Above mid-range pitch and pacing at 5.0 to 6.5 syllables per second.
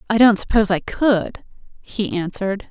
Yes: high, 205 Hz; 5.1 syllables/s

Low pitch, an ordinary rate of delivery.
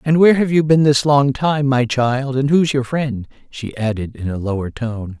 No: low, 130 Hz; fast, 230 wpm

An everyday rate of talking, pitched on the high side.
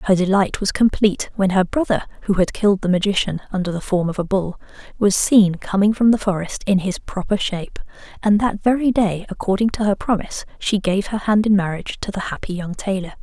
No: fast, 215 wpm; high, 195 Hz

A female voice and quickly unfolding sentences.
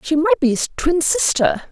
Yes: female; fast, 210 wpm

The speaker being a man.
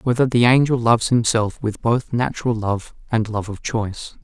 Yes: male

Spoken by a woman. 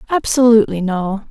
Yes: female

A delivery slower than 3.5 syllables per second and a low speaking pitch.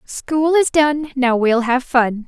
No: 3.3 syllables/s; very high, 270 Hz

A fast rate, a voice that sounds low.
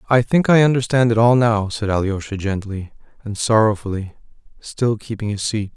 No: average, 165 wpm; low, 110 Hz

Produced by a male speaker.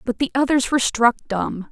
No: female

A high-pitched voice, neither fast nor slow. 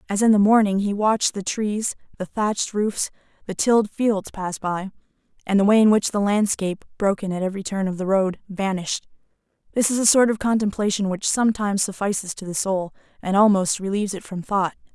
Yes: high, 200 Hz; average, 195 wpm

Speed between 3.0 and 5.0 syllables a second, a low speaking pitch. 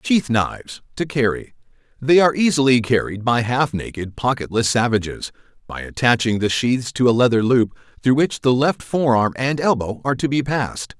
No: 5.2 syllables/s; low, 125 Hz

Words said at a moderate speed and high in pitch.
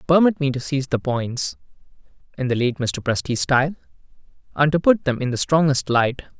No: average, 190 wpm; medium, 140 Hz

